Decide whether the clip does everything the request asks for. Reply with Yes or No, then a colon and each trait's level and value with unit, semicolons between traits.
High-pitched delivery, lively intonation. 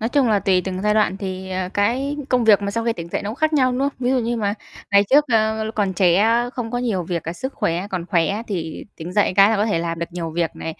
No: high, 205 Hz; average, 4.3 semitones